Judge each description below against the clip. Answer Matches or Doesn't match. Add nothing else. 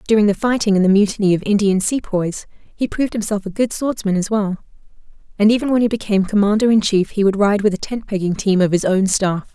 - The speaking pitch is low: Doesn't match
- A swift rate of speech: Matches